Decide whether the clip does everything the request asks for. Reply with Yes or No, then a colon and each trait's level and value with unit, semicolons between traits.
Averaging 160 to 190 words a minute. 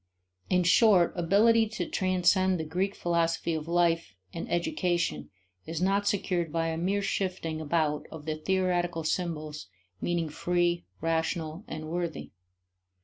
No: slow, 135 wpm